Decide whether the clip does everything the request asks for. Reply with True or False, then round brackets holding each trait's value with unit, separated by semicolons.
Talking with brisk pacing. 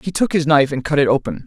True (325 wpm)